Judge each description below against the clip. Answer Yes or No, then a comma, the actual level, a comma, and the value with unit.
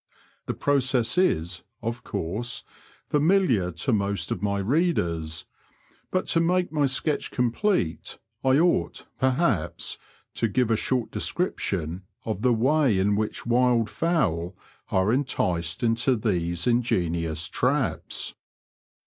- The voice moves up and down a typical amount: No, wide, 6.8 semitones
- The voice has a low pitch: Yes, low, 115 Hz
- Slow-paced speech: Yes, slow, 120 wpm